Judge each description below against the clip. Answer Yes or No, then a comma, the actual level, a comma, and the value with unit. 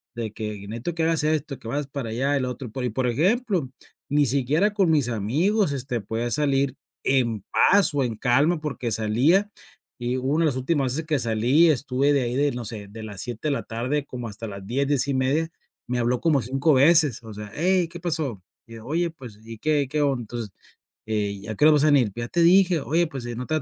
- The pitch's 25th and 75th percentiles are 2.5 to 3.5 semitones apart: No, average, 4.7 semitones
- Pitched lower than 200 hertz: Yes, low, 135 Hz